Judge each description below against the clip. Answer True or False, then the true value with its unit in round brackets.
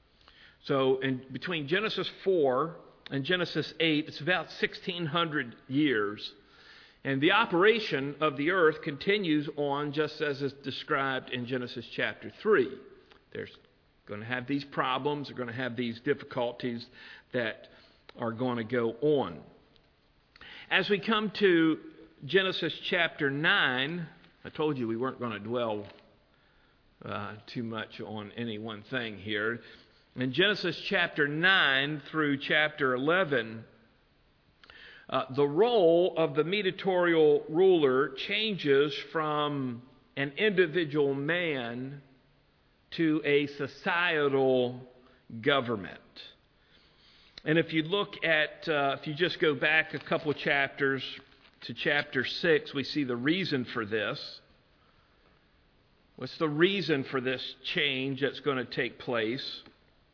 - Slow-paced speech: True (125 wpm)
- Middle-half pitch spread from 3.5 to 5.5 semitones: True (4.2 semitones)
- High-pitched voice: False (140 Hz)